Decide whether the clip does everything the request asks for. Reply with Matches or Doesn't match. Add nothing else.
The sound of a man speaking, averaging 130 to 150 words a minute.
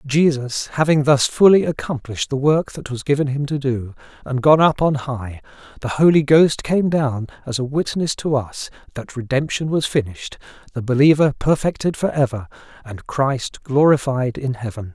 Doesn't match